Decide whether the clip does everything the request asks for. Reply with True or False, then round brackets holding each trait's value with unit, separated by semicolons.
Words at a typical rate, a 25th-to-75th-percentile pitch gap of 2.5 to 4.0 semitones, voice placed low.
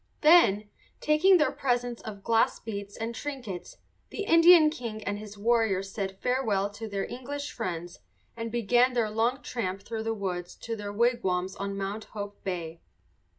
False (160 wpm; 3.7 semitones; 220 Hz)